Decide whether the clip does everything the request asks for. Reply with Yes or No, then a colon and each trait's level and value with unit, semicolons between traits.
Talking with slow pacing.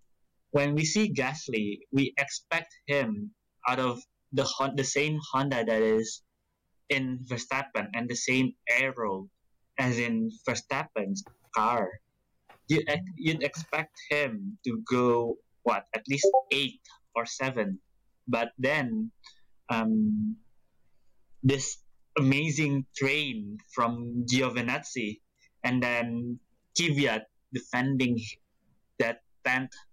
Yes: slow, 100 wpm